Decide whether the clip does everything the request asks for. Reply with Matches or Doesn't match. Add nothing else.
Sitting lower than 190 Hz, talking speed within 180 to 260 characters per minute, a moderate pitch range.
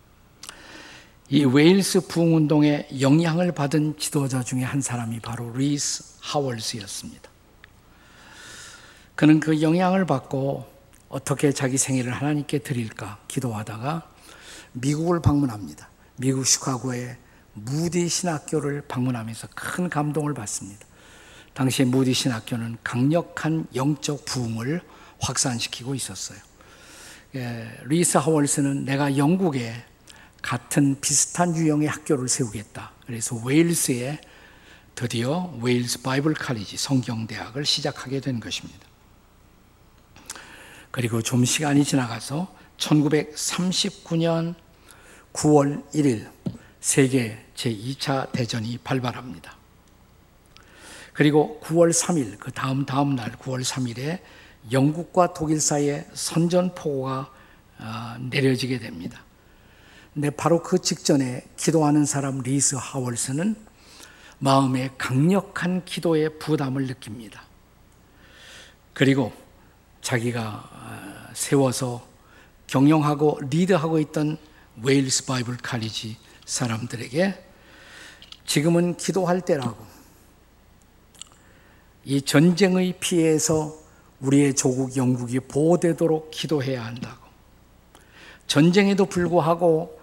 Matches